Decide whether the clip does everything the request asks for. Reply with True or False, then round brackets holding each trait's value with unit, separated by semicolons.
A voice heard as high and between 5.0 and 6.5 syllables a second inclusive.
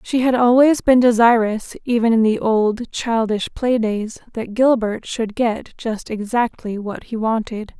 False (230 Hz; 4.1 syllables/s)